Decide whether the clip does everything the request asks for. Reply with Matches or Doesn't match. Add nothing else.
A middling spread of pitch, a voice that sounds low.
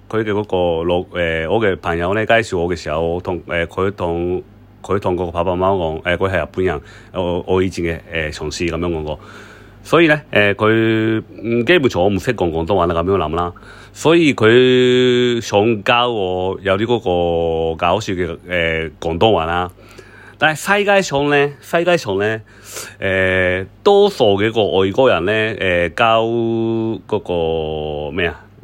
Matches